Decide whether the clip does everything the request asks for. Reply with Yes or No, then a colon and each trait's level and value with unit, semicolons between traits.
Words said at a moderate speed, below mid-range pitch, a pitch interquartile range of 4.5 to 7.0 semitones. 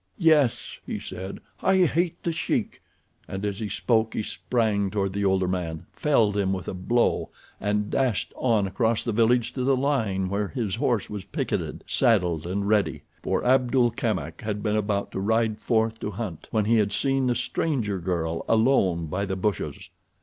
No: average, 180 wpm; low, 105 Hz; average, 3.9 semitones